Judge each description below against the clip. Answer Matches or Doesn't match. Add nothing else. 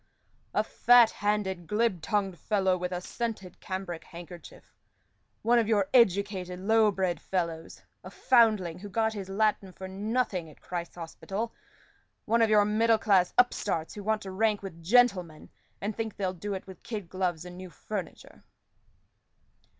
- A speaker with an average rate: Matches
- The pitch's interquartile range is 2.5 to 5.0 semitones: Matches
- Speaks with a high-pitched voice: Matches